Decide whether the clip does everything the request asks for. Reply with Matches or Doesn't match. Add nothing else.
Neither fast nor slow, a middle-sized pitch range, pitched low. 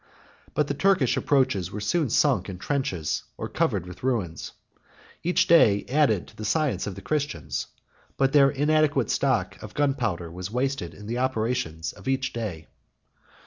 Doesn't match